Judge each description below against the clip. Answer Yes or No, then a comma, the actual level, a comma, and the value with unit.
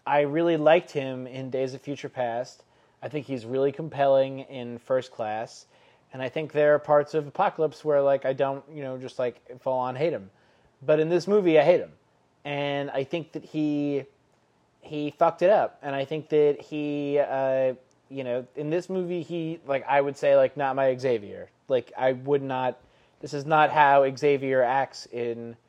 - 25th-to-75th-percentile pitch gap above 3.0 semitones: No, narrow, 2.5 semitones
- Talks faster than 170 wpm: Yes, average, 195 wpm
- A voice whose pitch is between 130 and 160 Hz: Yes, medium, 140 Hz